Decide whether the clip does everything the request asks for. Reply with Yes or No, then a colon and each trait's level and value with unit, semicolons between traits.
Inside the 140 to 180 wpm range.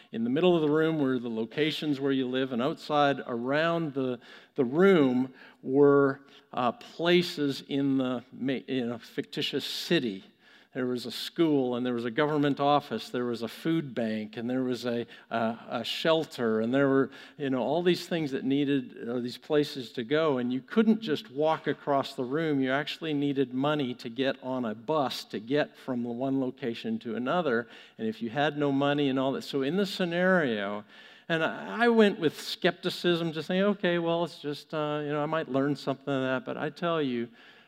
No: average, 200 wpm